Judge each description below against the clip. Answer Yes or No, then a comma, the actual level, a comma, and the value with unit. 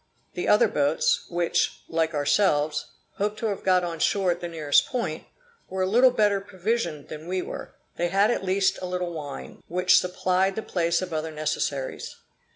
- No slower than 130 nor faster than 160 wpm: No, average, 180 wpm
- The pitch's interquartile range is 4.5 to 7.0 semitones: No, average, 3.4 semitones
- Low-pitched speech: No, medium, 180 Hz